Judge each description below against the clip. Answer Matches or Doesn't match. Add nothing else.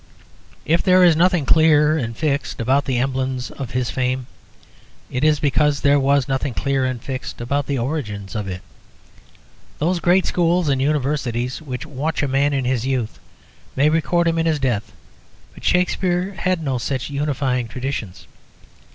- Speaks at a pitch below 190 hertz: Matches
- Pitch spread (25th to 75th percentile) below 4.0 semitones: Matches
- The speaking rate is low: Doesn't match